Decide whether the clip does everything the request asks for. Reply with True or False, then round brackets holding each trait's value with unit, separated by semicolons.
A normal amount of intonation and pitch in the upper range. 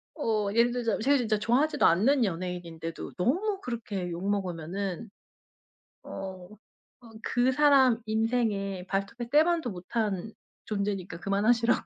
True (4.3 semitones; 215 Hz)